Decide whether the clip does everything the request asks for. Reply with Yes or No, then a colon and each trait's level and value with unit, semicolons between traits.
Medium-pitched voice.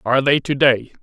No: low, 130 Hz